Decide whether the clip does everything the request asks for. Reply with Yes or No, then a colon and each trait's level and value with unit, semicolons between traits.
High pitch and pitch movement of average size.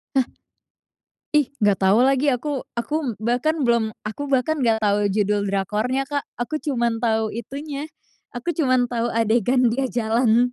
Yes: high, 240 Hz; average, 3.7 semitones